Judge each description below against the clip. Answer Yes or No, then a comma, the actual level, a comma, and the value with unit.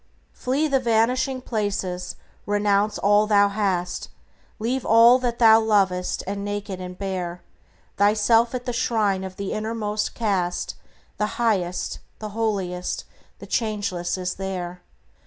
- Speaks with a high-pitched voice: Yes, high, 205 Hz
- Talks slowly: Yes, slow, 130 wpm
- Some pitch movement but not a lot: Yes, average, 3.1 semitones